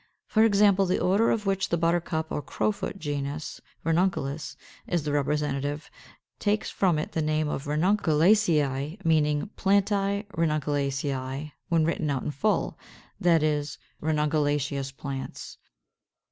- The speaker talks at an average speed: No, slow, 125 wpm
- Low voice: No, medium, 155 Hz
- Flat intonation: No, average, 4.4 semitones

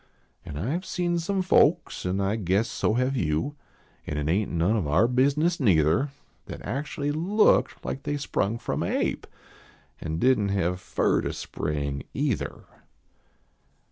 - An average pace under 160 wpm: No, average, 165 wpm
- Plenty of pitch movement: Yes, wide, 9.0 semitones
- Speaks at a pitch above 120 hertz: No, low, 110 Hz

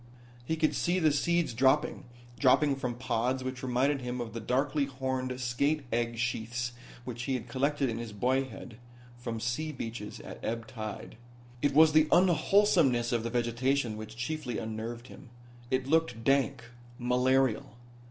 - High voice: No, low, 125 Hz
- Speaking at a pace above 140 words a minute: Yes, average, 155 wpm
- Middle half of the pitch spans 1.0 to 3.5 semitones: Yes, average, 3.0 semitones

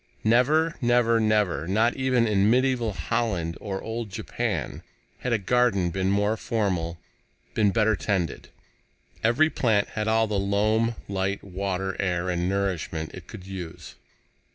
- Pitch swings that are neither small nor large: Yes, average, 3.4 semitones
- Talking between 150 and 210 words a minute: No, average, 140 wpm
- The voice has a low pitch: Yes, low, 105 Hz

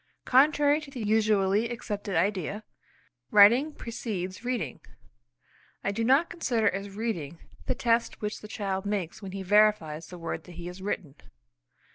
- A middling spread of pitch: Yes, average, 3.6 semitones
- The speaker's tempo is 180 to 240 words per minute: No, average, 150 wpm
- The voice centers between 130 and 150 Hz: No, high, 205 Hz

